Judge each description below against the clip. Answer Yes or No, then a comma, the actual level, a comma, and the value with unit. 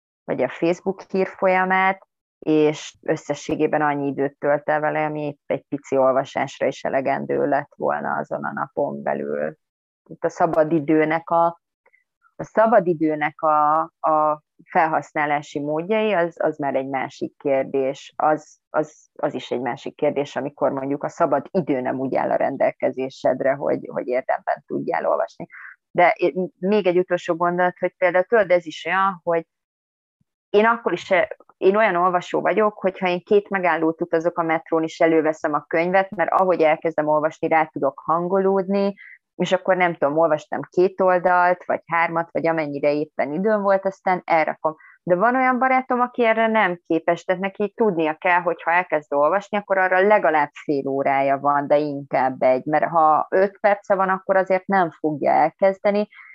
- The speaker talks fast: Yes, fast, 160 wpm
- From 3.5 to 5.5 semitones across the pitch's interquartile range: Yes, average, 3.9 semitones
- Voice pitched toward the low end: No, medium, 165 Hz